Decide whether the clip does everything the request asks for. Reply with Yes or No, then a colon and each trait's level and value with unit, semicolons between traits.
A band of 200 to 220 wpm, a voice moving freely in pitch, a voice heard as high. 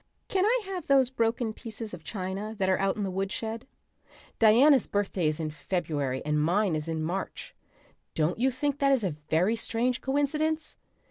No: average, 180 wpm; wide, 6.8 semitones; high, 215 Hz